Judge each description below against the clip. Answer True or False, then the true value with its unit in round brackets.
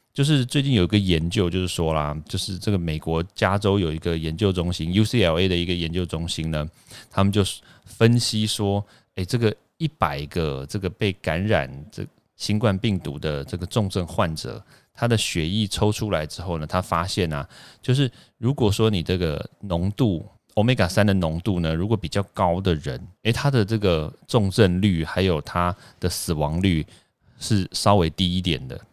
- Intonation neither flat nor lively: True (4.3 semitones)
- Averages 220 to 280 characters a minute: True (270 characters per minute)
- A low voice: True (95 Hz)